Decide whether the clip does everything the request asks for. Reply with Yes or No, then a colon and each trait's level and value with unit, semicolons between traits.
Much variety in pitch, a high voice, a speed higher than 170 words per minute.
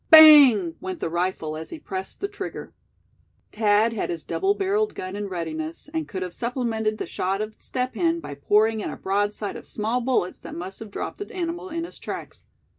Yes: wide, 6.2 semitones; high, 210 Hz; average, 200 wpm